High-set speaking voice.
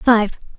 Yes: high, 220 Hz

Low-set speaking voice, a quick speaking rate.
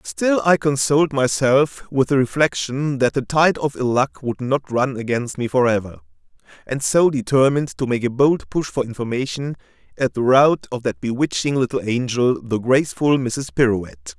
No: low, 130 Hz; average, 175 wpm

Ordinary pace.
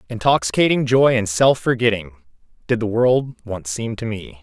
Yes: average, 165 wpm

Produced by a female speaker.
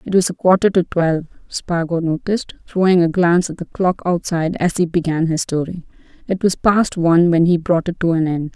Yes: female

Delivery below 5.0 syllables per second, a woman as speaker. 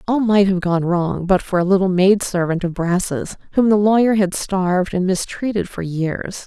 Yes: 4.6 syllables/s; female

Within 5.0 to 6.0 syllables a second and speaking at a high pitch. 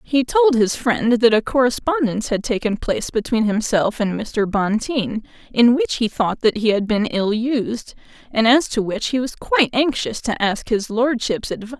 No: 4.8 syllables/s; high, 230 Hz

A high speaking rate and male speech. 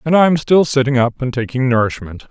Yes: fast, 210 wpm; male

